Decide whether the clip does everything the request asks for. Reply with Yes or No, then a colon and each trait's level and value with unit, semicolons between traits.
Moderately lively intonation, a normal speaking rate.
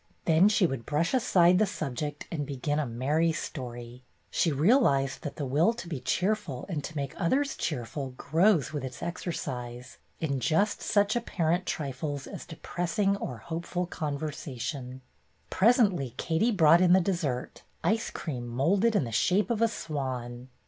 No: wide, 5.7 semitones; average, 155 wpm